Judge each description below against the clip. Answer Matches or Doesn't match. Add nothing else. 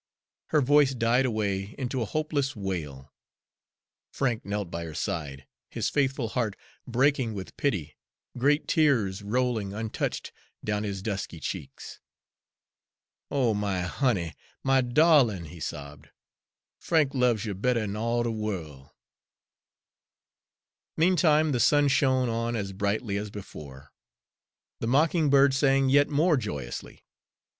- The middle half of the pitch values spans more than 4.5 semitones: Matches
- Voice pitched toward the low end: Matches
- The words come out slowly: Matches